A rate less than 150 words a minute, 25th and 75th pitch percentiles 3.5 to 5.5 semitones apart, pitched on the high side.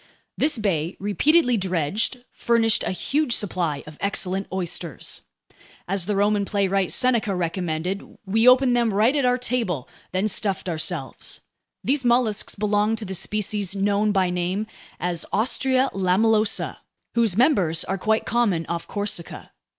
Yes: average, 140 wpm; average, 4.0 semitones; high, 205 Hz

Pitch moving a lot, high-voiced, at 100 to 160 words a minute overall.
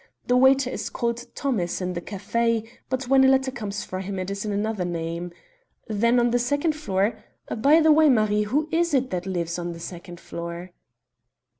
No: wide, 6.0 semitones; high, 220 Hz; average, 195 wpm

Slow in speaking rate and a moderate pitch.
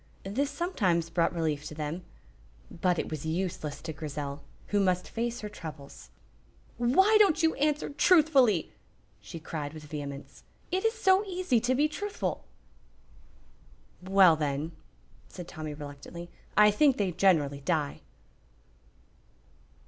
Yes: slow, 130 wpm; medium, 180 Hz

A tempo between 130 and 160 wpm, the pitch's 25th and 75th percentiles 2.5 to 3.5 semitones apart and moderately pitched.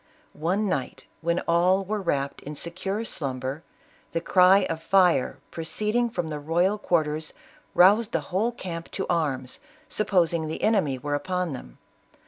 No: average, 150 wpm; average, 4.2 semitones; medium, 170 Hz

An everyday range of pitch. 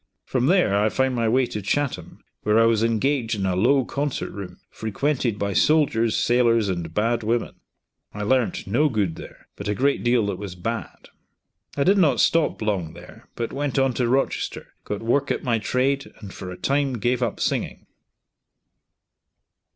Yes: average, 4.4 semitones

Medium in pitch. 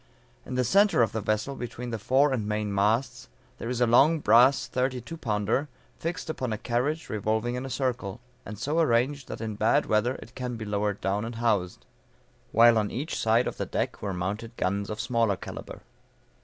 No: low, 115 Hz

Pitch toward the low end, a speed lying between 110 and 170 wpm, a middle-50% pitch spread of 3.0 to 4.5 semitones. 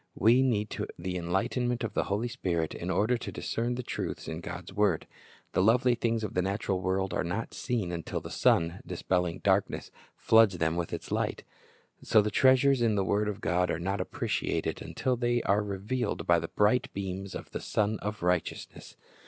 No: low, 100 Hz; average, 195 wpm; average, 4.2 semitones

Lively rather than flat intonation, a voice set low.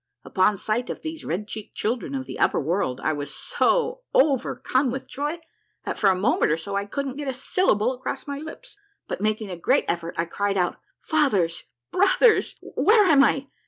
No: wide, 7.1 semitones; high, 245 Hz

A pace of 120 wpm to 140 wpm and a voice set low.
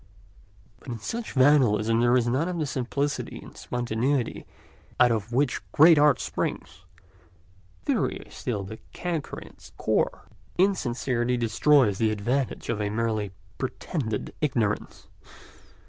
Yes: slow, 135 wpm; low, 120 Hz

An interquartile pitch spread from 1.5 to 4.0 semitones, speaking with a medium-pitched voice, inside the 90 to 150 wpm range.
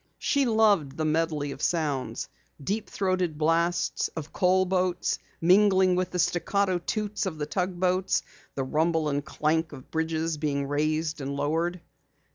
Yes: average, 3.3 semitones; medium, 165 Hz; average, 145 wpm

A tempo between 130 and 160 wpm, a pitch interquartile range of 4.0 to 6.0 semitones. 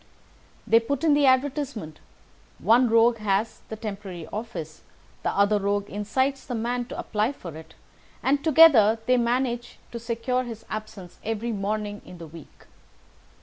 No: average, 150 wpm; average, 3.5 semitones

